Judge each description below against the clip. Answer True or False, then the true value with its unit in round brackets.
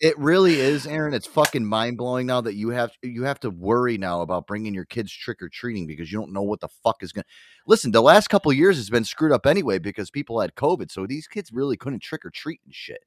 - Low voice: True (120 Hz)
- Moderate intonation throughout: False (6.4 semitones)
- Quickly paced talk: True (250 wpm)